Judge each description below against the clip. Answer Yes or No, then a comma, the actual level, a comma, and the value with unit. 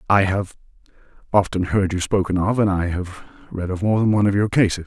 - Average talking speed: No, fast, 220 wpm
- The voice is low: Yes, very low, 95 Hz